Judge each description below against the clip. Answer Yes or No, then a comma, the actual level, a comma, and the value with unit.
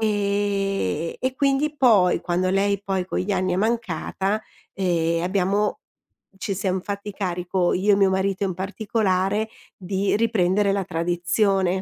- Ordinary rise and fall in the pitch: No, narrow, 2.2 semitones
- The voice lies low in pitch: No, high, 195 Hz